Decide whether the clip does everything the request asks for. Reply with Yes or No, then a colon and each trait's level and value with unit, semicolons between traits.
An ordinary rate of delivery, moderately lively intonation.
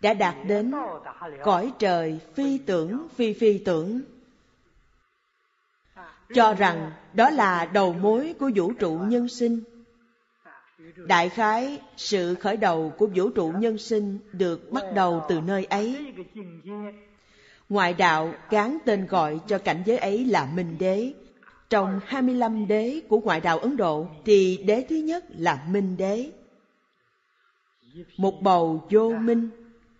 No: slow, 135 wpm; average, 4.2 semitones